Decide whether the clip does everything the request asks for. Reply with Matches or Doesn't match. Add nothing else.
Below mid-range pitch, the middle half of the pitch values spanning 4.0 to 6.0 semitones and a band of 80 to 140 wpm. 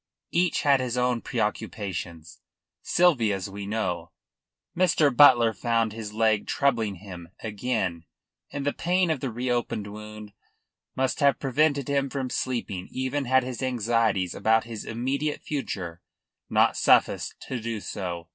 Matches